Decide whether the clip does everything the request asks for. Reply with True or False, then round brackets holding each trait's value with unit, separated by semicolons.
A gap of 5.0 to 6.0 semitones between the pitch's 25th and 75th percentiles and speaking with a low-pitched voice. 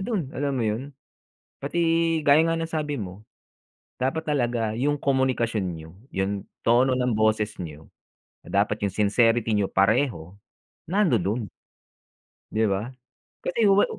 True (5.5 semitones; 120 Hz)